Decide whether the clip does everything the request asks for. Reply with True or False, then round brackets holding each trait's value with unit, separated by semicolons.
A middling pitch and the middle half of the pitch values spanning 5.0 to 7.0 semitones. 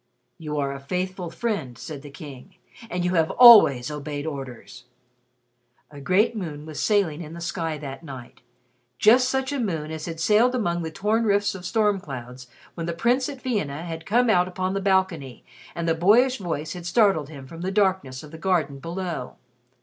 True (170 Hz; 5.3 semitones)